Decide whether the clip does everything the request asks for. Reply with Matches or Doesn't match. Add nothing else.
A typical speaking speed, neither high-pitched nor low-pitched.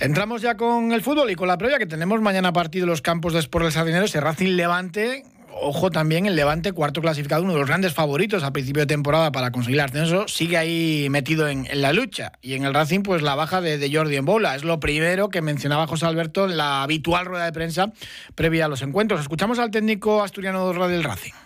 Doesn't match